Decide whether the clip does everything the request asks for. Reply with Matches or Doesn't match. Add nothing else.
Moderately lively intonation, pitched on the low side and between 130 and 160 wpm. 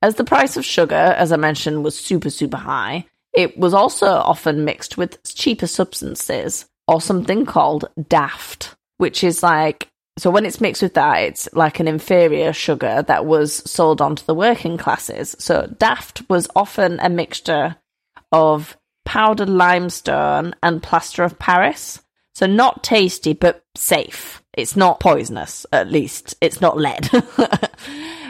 Doesn't match